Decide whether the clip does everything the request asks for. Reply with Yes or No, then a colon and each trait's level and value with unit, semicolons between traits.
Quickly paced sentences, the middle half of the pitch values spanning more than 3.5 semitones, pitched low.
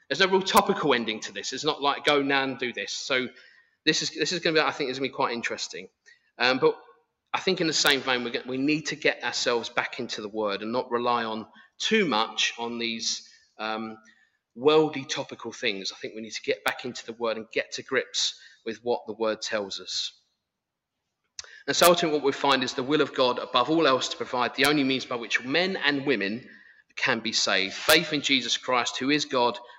Yes: fast, 230 wpm; average, 4.5 semitones; low, 130 Hz